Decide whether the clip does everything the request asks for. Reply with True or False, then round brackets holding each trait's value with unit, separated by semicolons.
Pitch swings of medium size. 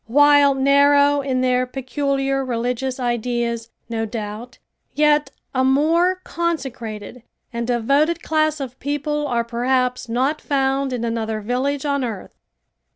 True (3.1 semitones)